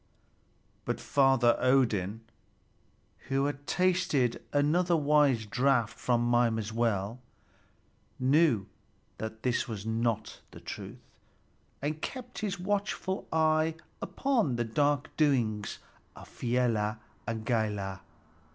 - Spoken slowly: Yes, slow, 105 wpm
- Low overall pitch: Yes, low, 125 Hz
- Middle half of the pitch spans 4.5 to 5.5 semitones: Yes, average, 5.2 semitones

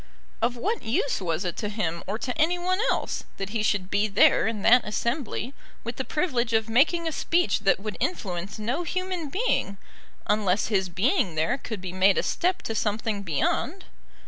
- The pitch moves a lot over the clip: Yes, wide, 6.5 semitones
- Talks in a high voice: Yes, high, 225 Hz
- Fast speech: No, average, 190 wpm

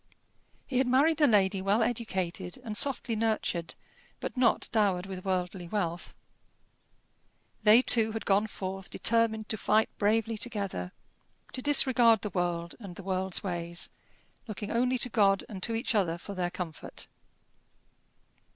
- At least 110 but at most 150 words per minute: Yes, average, 145 wpm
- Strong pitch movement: No, average, 3.7 semitones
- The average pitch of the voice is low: No, high, 205 Hz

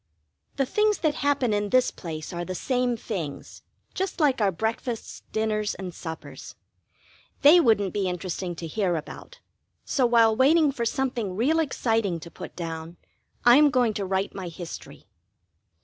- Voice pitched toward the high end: Yes, high, 220 Hz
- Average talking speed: Yes, average, 160 wpm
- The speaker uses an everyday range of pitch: No, wide, 6.3 semitones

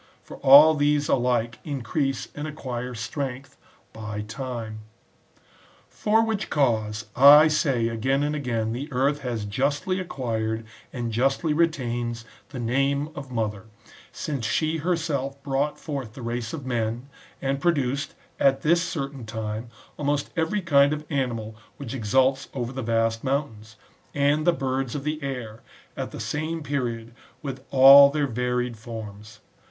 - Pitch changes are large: No, average, 3.9 semitones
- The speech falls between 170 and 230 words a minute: No, average, 145 wpm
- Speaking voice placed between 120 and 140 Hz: Yes, low, 135 Hz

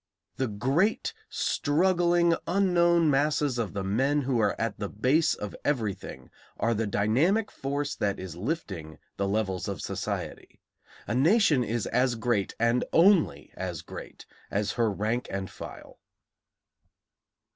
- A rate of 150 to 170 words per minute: No, slow, 135 wpm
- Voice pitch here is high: No, low, 125 Hz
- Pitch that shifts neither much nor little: No, wide, 7.4 semitones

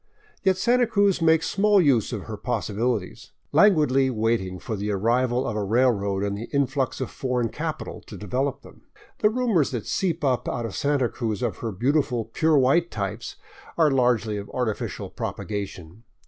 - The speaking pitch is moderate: No, low, 125 Hz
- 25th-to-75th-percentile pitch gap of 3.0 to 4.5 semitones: No, wide, 5.6 semitones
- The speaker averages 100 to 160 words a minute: No, average, 170 wpm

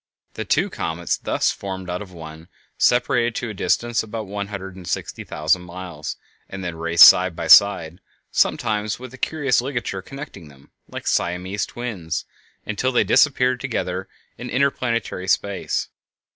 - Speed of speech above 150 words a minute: Yes, average, 160 wpm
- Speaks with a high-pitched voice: No, very low, 95 Hz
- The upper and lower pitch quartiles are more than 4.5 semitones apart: Yes, average, 5.3 semitones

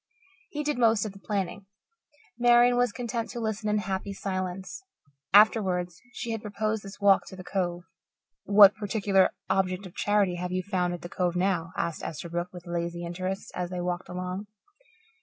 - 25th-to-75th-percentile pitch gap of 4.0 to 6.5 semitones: No, average, 2.9 semitones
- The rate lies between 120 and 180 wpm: Yes, average, 175 wpm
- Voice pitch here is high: Yes, high, 195 Hz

